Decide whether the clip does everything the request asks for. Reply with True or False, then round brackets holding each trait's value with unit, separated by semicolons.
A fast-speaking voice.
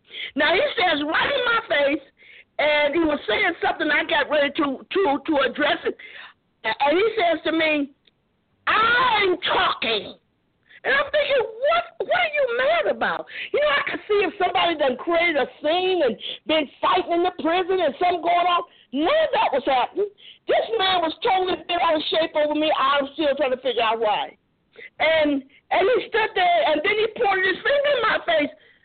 False (195 wpm)